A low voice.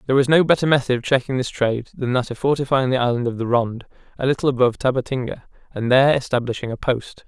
Yes: low, 130 Hz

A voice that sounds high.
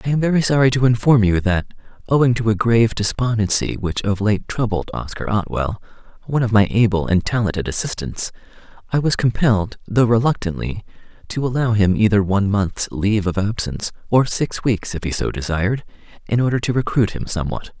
No: low, 110 Hz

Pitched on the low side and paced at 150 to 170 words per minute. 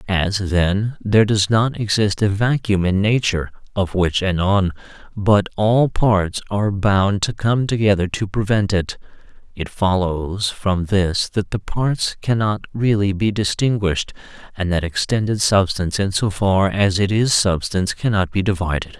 Yes: low, 100 Hz; average, 155 wpm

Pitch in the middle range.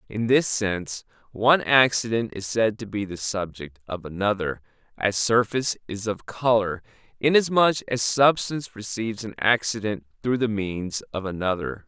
No: low, 105 Hz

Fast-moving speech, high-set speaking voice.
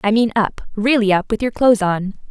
Yes: fast, 210 wpm; high, 215 Hz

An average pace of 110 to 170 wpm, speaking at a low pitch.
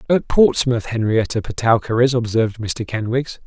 Yes: average, 140 wpm; low, 120 Hz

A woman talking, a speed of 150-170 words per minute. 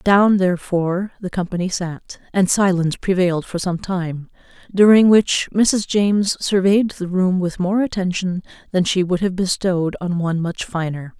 Yes: female; average, 160 wpm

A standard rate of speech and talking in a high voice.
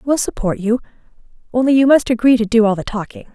No: fast, 215 wpm; high, 230 Hz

